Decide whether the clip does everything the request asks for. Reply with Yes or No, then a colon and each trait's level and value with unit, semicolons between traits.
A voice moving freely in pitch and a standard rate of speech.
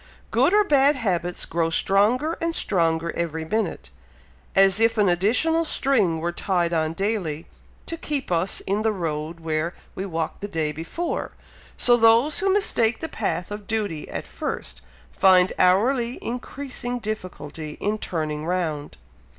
Yes: wide, 6.3 semitones; average, 150 wpm